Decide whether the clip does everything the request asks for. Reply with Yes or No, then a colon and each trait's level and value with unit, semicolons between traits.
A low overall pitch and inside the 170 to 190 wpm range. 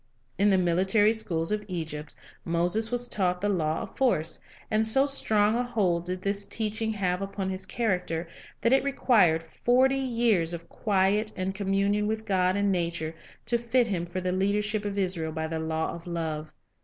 No: high, 195 Hz; average, 180 wpm